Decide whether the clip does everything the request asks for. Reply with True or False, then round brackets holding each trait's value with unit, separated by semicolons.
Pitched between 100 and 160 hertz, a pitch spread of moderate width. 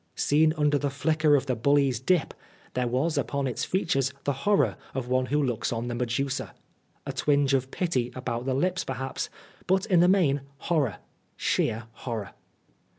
True (135 Hz; 3.3 semitones)